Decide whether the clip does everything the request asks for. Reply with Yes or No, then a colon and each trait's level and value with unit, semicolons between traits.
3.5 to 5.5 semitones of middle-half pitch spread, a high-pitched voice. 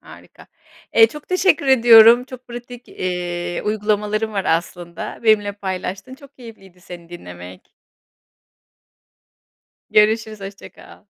Yes: average, 4.8 semitones; high, 210 Hz